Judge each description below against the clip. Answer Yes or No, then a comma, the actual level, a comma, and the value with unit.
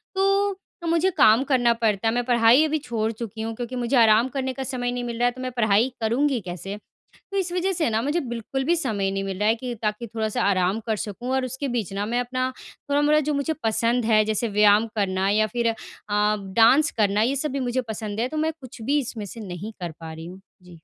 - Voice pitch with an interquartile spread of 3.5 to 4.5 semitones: Yes, average, 3.8 semitones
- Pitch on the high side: Yes, high, 235 Hz